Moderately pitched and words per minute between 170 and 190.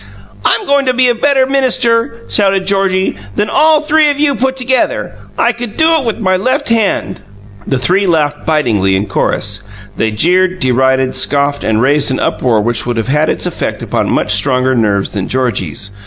Yes: medium, 180 Hz; average, 185 wpm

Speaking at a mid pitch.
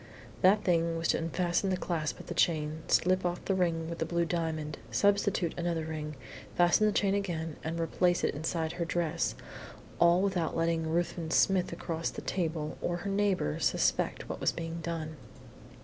Yes: medium, 170 Hz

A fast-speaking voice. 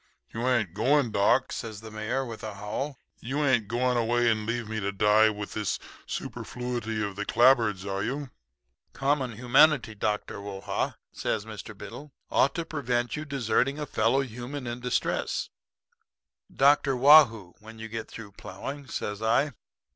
No: average, 165 wpm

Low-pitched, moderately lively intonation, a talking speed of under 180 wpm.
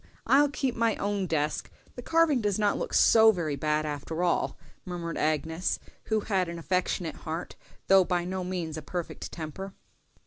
No: medium, 180 Hz; average, 4.2 semitones; average, 170 wpm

